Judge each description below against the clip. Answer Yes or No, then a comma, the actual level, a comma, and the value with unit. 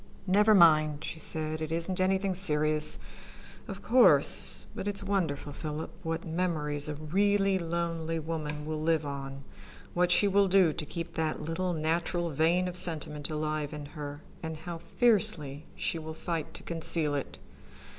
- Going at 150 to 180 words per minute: Yes, average, 155 wpm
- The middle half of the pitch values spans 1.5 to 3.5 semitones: Yes, average, 2.9 semitones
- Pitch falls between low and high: Yes, medium, 160 Hz